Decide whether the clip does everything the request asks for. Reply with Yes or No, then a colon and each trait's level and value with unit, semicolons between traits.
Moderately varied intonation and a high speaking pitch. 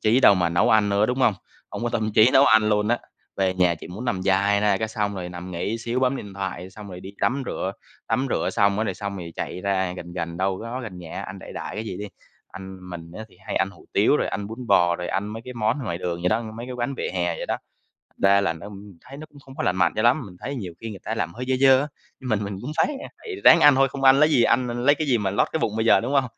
No: average, 4.7 semitones; low, 105 Hz